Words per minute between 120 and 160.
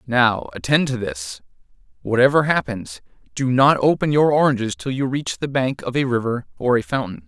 No: average, 180 wpm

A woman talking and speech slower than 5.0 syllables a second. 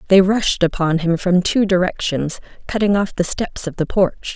Yes: female; 4.7 syllables/s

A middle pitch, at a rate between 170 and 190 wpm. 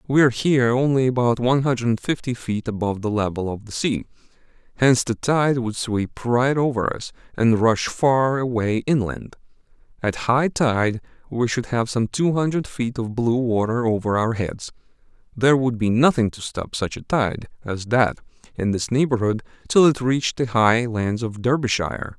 No: low, 120 Hz; average, 180 wpm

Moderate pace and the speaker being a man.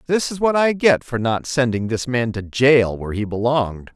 No: fast, 225 wpm; male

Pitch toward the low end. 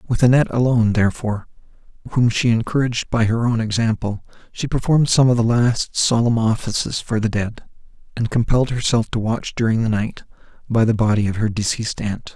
Yes: low, 115 Hz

